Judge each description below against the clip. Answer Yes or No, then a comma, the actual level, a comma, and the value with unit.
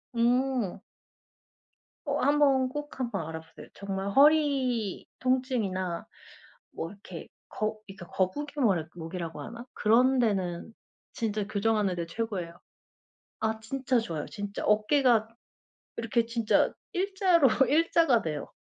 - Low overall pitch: No, high, 225 Hz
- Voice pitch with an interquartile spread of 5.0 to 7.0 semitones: Yes, wide, 5.5 semitones